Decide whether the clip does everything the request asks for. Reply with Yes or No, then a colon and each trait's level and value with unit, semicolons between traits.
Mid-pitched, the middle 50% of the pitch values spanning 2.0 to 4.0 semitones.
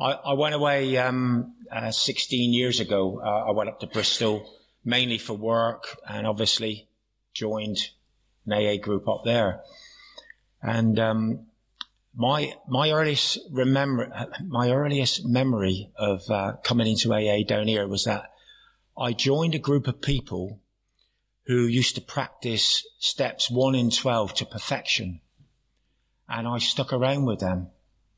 No: low, 115 Hz; average, 3.3 semitones